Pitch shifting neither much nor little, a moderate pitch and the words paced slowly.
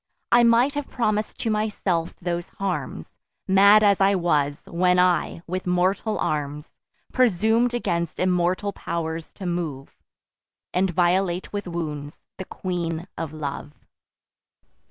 Yes: average, 3.3 semitones; medium, 180 Hz; slow, 125 wpm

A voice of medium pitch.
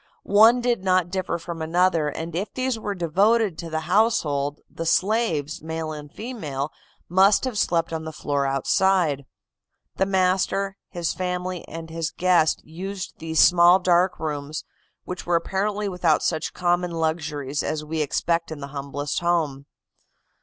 Yes: medium, 170 Hz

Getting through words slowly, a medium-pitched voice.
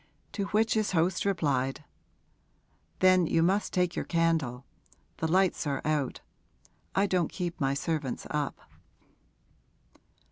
Yes: slow, 120 wpm; medium, 165 Hz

